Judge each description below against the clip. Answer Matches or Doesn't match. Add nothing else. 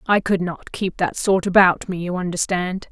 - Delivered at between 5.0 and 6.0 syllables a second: Doesn't match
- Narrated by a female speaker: Matches